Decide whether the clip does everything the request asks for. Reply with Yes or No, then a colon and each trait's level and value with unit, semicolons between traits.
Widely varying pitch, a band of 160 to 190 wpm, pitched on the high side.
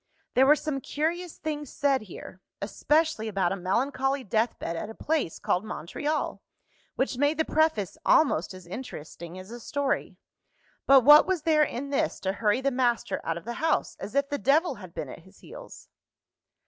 Yes: wide, 6.4 semitones; average, 180 wpm; very high, 265 Hz